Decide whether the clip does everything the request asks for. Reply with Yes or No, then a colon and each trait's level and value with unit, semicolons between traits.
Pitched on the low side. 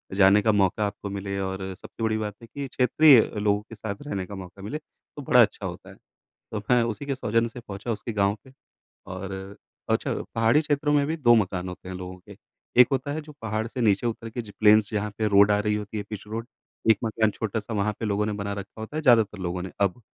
Yes: low, 105 Hz